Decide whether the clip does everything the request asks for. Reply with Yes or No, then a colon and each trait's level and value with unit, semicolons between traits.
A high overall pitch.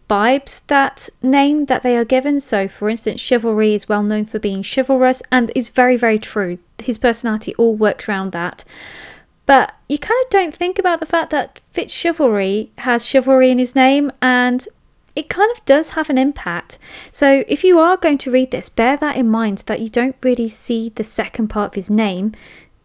Yes: very high, 250 Hz